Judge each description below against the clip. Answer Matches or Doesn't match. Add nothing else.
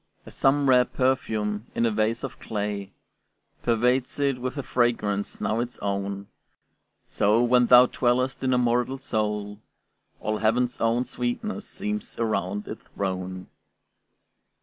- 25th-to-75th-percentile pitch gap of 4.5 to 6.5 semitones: Doesn't match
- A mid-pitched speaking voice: Doesn't match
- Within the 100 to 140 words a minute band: Matches